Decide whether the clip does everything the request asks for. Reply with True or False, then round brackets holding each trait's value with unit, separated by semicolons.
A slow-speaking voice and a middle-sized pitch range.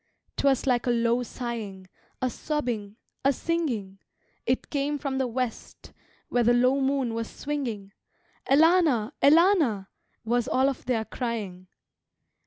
True (130 wpm; 3.5 semitones)